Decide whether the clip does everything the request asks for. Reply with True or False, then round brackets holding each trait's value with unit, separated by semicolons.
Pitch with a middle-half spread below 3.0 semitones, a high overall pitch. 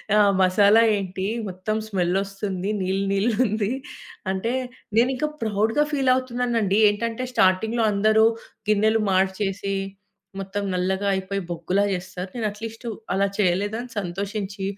True (2.6 semitones; 200 Hz)